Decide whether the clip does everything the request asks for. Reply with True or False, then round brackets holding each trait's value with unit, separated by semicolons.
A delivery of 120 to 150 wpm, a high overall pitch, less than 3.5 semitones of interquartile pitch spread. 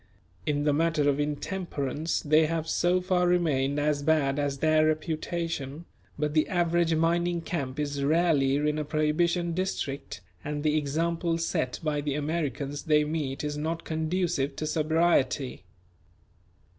False (145 wpm; 155 Hz; 2.5 semitones)